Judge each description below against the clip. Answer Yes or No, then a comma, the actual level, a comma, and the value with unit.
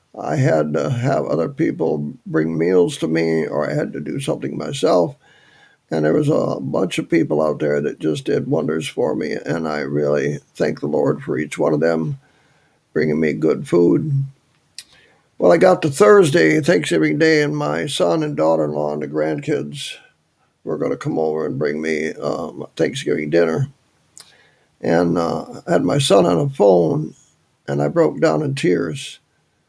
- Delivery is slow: No, average, 180 wpm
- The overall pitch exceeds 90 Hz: No, very low, 80 Hz